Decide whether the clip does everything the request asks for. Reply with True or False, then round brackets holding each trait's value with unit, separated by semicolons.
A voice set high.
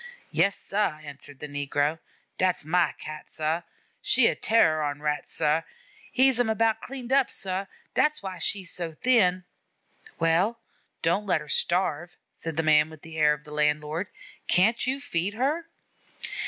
False (175 Hz)